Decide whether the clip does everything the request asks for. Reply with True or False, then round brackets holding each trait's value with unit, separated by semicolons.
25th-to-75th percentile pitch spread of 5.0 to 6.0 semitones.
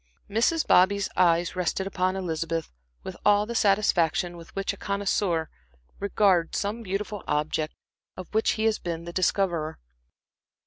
False (3.2 semitones)